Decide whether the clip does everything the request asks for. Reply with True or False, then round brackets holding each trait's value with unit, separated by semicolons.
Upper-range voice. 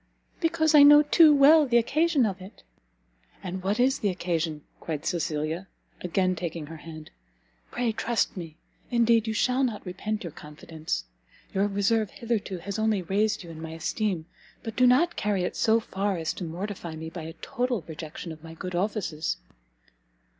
True (195 Hz)